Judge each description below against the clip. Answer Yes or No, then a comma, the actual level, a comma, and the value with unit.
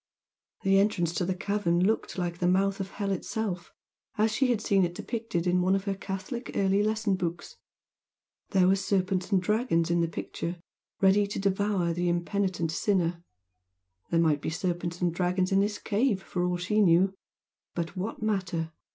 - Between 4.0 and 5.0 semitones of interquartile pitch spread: No, narrow, 2.5 semitones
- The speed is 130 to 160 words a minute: No, average, 175 wpm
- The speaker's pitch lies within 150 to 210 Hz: Yes, high, 190 Hz